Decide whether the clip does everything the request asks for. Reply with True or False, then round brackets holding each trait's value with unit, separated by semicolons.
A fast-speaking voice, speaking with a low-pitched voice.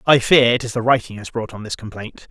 True (285 wpm; 120 Hz)